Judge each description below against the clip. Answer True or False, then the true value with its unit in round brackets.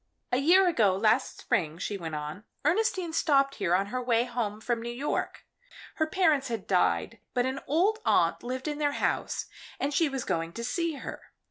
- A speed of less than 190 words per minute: False (195 wpm)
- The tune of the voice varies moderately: False (6.5 semitones)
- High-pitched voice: True (255 Hz)